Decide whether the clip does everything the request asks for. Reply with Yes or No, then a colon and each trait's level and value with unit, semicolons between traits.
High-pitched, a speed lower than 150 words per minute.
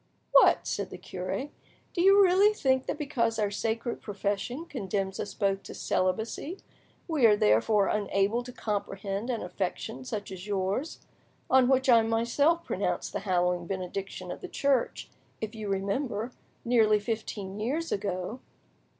Yes: high, 215 Hz; average, 140 wpm